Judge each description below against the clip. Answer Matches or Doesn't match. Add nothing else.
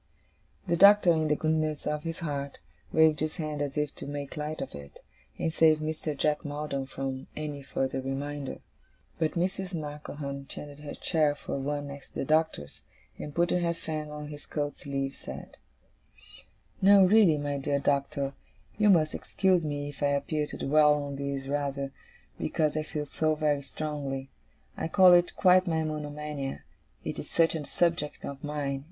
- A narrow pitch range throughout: Matches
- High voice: Doesn't match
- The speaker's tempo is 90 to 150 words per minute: Doesn't match